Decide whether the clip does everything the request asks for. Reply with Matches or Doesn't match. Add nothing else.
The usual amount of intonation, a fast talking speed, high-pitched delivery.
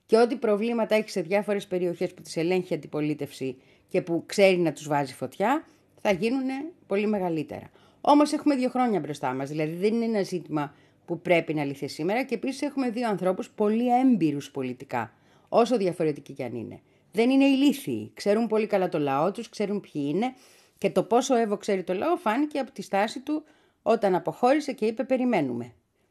Doesn't match